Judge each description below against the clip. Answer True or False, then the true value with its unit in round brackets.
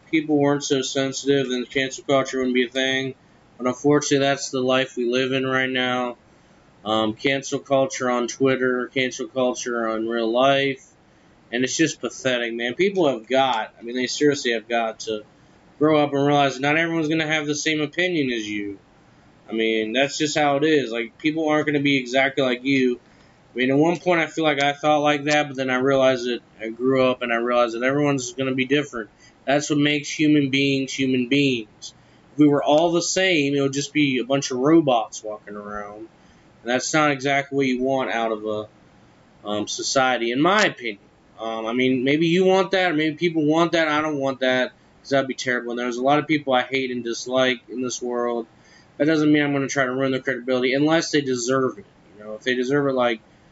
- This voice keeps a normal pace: False (225 wpm)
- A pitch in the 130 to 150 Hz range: True (135 Hz)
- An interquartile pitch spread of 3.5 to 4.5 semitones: False (2.9 semitones)